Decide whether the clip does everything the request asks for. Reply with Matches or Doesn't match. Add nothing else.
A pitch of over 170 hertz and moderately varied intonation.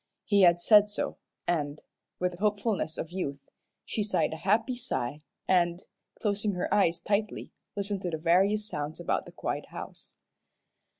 Matches